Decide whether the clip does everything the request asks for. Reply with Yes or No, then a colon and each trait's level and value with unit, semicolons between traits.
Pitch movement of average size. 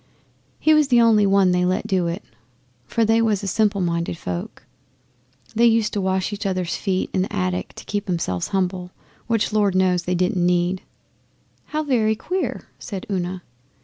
Yes: average, 3.3 semitones